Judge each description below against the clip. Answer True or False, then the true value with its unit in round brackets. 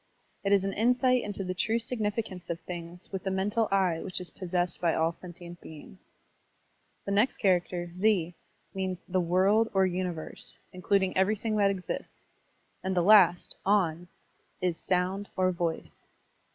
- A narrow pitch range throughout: True (2.3 semitones)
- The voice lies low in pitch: False (185 Hz)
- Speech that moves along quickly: False (160 wpm)